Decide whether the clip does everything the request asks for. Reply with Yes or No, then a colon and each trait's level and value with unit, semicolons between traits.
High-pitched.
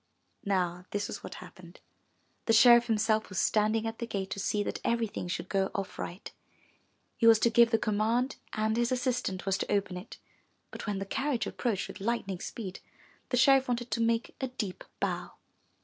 Yes: high, 220 Hz